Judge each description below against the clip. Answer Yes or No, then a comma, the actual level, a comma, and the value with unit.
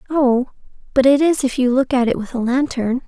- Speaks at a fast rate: Yes, fast, 235 wpm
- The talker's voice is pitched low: No, very high, 260 Hz